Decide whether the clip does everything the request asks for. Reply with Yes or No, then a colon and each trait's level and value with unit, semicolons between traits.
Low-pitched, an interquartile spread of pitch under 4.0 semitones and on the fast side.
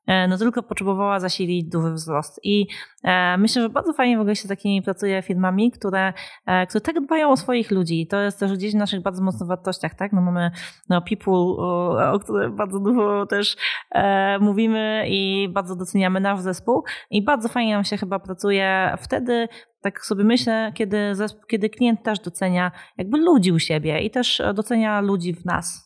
No: high, 200 Hz; average, 2.7 semitones; fast, 185 wpm